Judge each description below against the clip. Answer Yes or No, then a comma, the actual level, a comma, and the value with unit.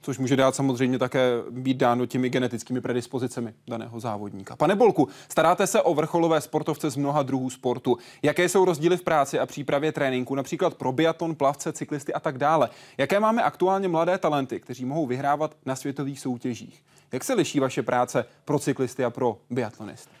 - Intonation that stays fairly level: No, average, 3.6 semitones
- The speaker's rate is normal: No, fast, 180 wpm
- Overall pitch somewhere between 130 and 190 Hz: Yes, low, 135 Hz